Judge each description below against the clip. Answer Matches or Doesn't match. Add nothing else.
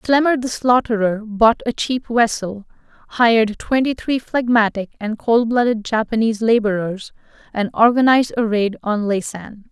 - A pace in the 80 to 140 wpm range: Matches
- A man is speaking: Doesn't match